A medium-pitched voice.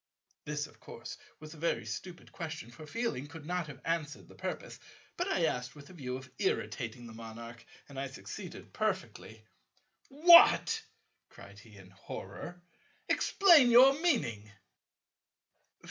Yes: medium, 150 Hz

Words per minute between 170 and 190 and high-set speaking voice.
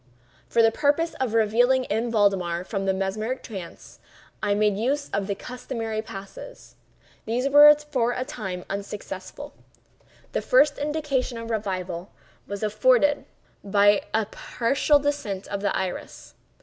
No: slow, 135 wpm; high, 220 Hz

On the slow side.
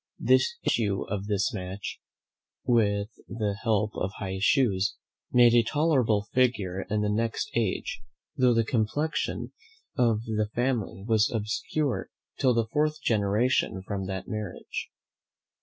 Yes: slow, 130 wpm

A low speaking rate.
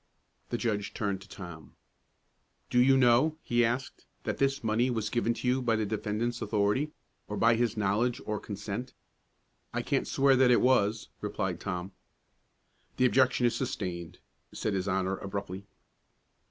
No: average, 155 wpm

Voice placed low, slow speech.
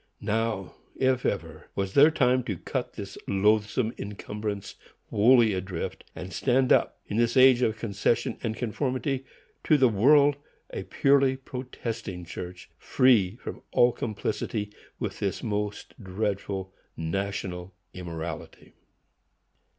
Yes: low, 110 Hz; slow, 120 wpm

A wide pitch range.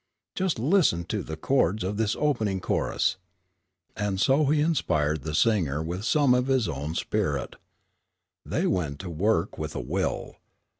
Yes: wide, 8.5 semitones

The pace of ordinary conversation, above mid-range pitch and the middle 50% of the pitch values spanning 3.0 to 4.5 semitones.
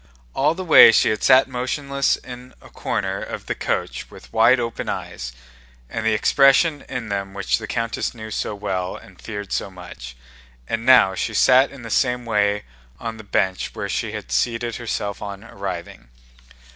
No: average, 180 wpm; low, 110 Hz; average, 3.9 semitones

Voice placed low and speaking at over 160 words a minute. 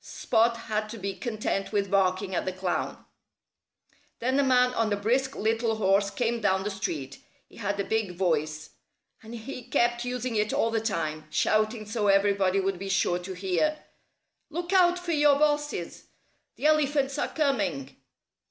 No: high, 215 Hz; average, 170 wpm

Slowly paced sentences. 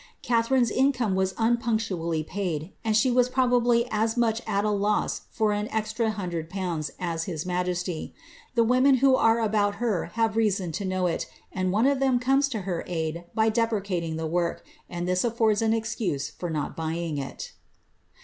No: average, 180 wpm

